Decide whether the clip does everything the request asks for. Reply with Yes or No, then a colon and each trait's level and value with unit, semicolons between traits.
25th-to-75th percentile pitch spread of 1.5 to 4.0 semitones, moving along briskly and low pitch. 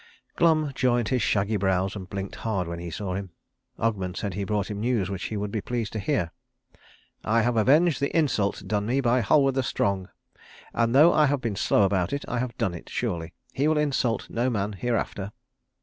No: average, 4.5 semitones; fast, 210 wpm; low, 110 Hz